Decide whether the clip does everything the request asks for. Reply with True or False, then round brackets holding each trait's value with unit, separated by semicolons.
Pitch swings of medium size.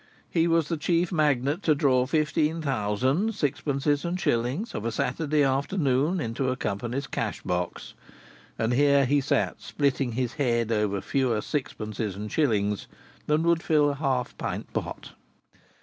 True (4.4 semitones)